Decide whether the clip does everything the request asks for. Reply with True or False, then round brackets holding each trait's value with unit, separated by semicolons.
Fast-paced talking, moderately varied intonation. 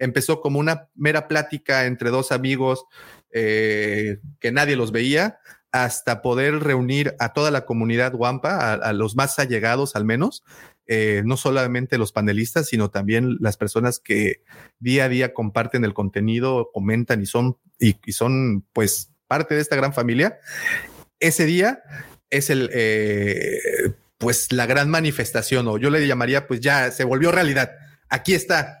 False (160 wpm; 4.1 semitones)